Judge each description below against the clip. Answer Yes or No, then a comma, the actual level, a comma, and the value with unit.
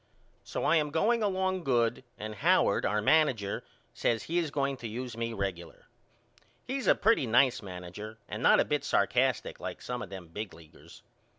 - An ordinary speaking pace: Yes, average, 180 wpm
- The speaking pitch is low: Yes, low, 125 Hz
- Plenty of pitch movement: Yes, wide, 6.5 semitones